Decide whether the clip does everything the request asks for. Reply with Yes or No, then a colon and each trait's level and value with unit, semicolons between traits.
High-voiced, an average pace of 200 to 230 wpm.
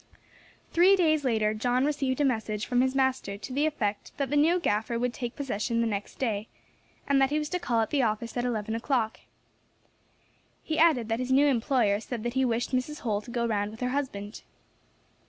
Yes: high, 245 Hz; fast, 205 wpm